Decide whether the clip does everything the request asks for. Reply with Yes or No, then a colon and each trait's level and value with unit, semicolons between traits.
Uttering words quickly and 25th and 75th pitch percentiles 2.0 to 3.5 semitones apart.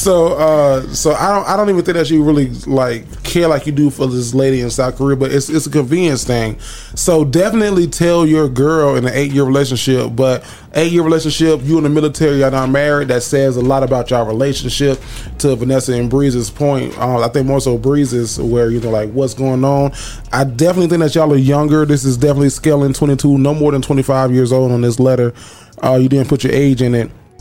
Yes: fast, 225 wpm; average, 2.9 semitones